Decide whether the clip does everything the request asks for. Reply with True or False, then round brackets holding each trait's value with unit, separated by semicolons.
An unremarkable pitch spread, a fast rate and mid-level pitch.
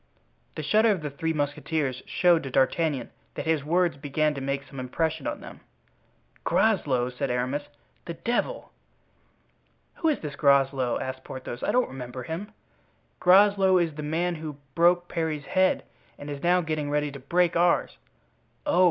False (4.1 semitones; 160 wpm; 155 Hz)